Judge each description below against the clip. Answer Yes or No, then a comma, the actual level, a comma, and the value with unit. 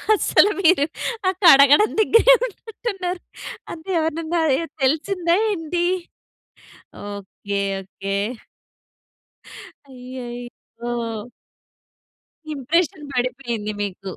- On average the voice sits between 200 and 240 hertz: No, very high, 280 Hz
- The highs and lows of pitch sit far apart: Yes, wide, 6.6 semitones